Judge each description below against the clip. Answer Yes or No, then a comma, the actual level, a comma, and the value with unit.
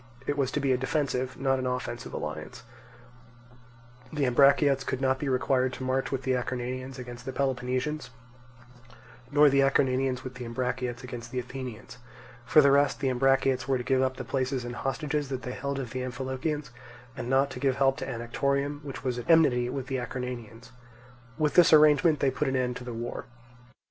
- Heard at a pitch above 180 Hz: No, low, 130 Hz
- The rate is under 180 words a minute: No, average, 190 wpm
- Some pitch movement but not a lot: No, narrow, 1.6 semitones